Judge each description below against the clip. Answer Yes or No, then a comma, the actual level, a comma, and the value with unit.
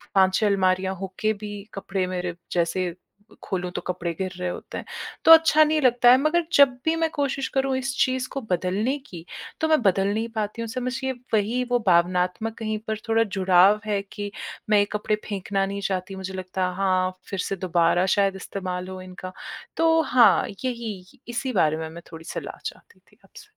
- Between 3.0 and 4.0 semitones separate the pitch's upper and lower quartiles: No, average, 5.0 semitones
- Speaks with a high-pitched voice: Yes, high, 200 Hz